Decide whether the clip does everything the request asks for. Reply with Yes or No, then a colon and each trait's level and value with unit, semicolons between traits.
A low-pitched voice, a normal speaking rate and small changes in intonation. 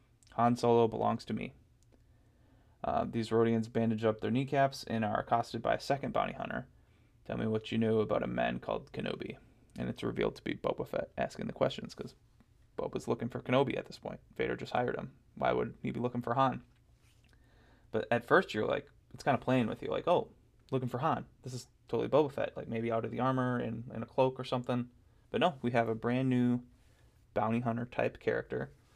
No: low, 120 Hz; fast, 215 wpm; narrow, 1.8 semitones